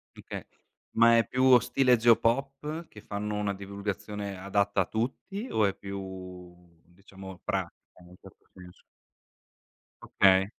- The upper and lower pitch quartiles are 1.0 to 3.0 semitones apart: No, average, 3.5 semitones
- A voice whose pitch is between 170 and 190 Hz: No, low, 100 Hz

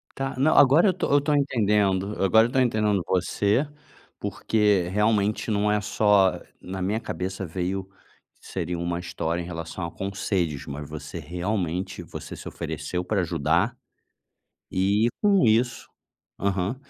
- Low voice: Yes, low, 100 Hz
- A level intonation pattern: No, average, 3.8 semitones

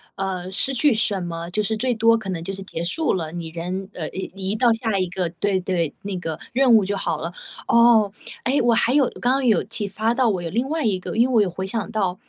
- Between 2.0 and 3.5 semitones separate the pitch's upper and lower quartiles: No, average, 4.3 semitones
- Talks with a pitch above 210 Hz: No, high, 200 Hz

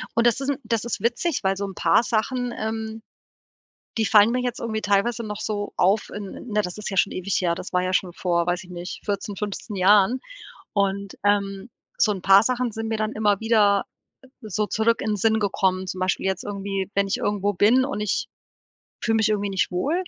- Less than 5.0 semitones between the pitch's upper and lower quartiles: Yes, narrow, 2.4 semitones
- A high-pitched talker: Yes, high, 205 Hz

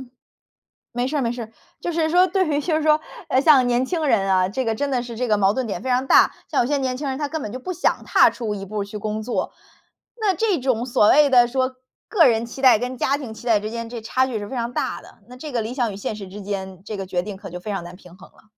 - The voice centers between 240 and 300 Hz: Yes, high, 245 Hz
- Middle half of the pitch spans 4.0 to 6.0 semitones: Yes, average, 4.3 semitones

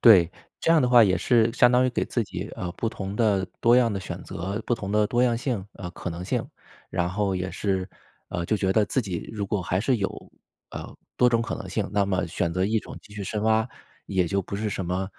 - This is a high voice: No, low, 100 Hz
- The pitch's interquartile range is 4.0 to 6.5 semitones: No, average, 3.5 semitones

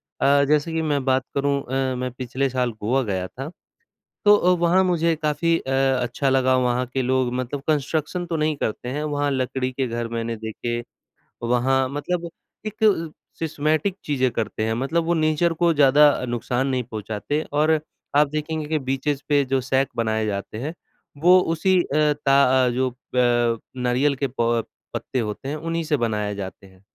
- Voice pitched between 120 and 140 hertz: Yes, low, 135 Hz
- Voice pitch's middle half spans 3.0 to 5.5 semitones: Yes, average, 3.8 semitones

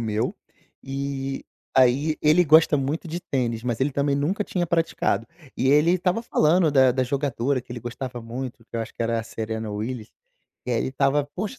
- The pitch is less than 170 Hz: Yes, low, 135 Hz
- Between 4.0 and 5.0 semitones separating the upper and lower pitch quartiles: Yes, average, 4.4 semitones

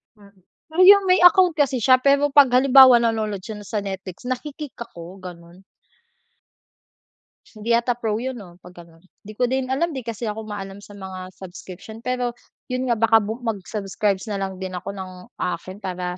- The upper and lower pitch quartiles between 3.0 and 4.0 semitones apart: No, average, 5.0 semitones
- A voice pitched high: Yes, high, 215 Hz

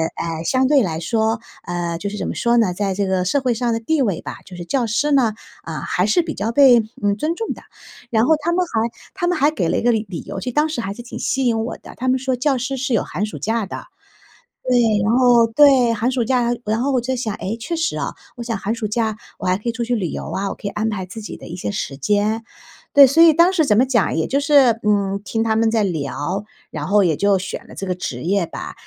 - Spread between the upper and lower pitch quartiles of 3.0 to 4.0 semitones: No, average, 4.6 semitones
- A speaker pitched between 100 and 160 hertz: No, high, 225 Hz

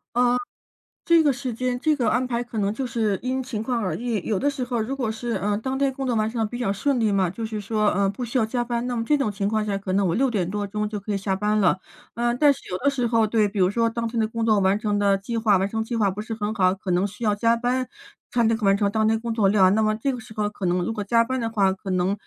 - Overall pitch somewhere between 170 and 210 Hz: No, high, 220 Hz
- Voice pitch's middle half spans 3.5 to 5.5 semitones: No, average, 3.0 semitones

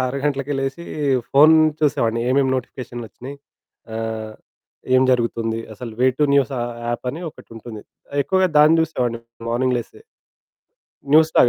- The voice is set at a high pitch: No, low, 130 Hz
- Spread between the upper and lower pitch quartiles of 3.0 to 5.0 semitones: Yes, average, 3.6 semitones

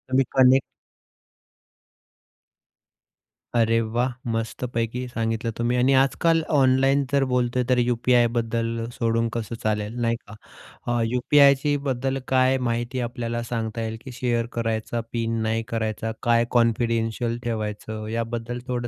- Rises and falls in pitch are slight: Yes, narrow, 1.8 semitones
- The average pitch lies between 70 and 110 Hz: No, low, 120 Hz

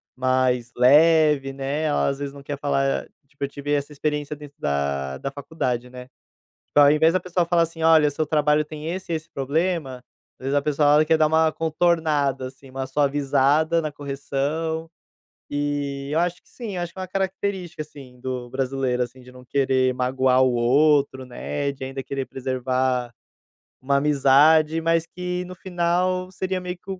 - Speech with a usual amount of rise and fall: Yes, average, 3.5 semitones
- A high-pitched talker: No, medium, 145 Hz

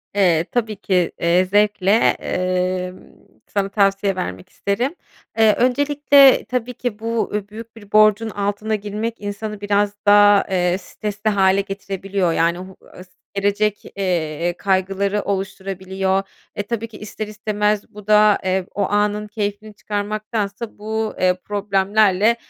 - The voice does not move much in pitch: Yes, narrow, 1.8 semitones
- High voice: Yes, high, 205 Hz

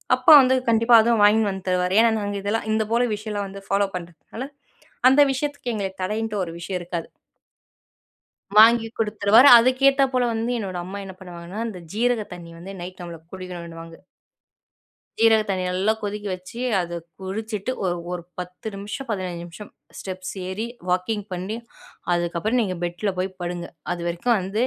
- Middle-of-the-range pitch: No, high, 200 Hz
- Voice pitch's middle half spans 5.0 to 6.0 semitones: No, average, 3.7 semitones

